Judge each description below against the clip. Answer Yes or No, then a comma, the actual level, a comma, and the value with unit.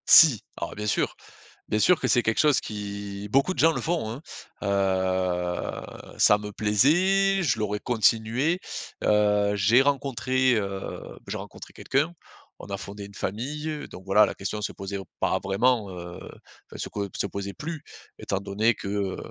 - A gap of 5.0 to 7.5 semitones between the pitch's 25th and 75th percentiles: Yes, average, 5.3 semitones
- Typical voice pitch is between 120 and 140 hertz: No, low, 105 Hz